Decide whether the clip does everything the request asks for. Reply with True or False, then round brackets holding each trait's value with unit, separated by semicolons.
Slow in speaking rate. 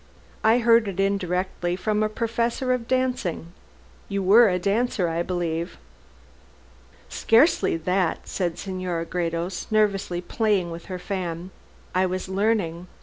True (130 wpm)